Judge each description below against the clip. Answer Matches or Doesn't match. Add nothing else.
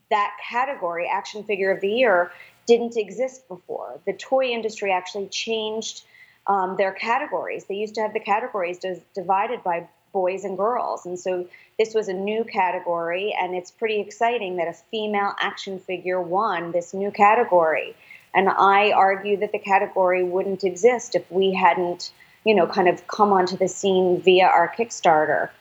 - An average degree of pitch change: Matches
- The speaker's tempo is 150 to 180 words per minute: Matches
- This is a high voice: Matches